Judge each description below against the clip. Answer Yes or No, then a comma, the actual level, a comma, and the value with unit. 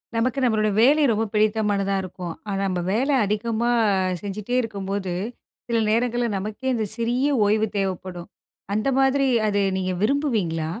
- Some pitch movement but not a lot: Yes, average, 3.5 semitones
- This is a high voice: Yes, high, 215 Hz